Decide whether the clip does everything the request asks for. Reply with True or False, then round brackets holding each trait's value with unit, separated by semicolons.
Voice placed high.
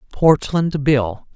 False (155 Hz)